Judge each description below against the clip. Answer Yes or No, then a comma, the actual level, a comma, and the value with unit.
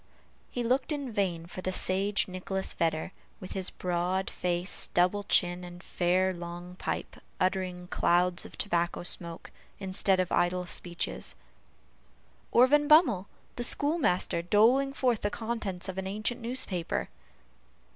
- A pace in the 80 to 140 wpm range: Yes, slow, 135 wpm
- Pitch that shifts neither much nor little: Yes, average, 3.5 semitones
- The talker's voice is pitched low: No, medium, 185 Hz